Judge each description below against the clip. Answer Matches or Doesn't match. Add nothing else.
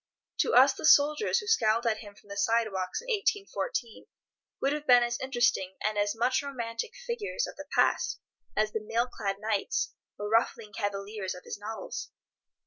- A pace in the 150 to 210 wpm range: Matches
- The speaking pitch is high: Matches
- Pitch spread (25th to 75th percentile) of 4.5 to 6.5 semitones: Matches